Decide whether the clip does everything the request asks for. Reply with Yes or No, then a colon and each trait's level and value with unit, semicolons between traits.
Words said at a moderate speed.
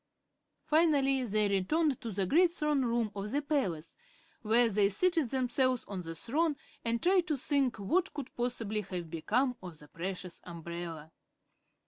Yes: average, 155 wpm